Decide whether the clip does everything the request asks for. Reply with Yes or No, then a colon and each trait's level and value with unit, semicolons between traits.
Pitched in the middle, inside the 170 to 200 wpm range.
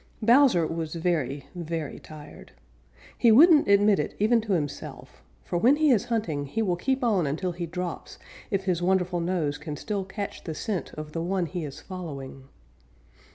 Yes: medium, 180 Hz; average, 180 wpm